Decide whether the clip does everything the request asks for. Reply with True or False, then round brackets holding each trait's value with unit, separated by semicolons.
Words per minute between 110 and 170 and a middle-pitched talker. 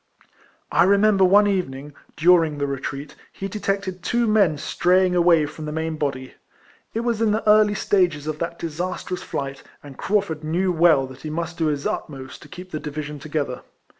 False (180 wpm; 165 Hz)